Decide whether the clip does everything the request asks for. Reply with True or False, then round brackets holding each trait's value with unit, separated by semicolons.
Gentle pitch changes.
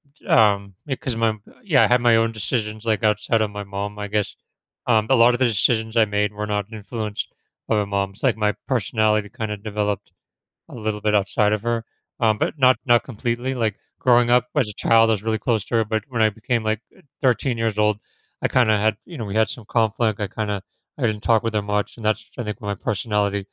True (2.0 semitones)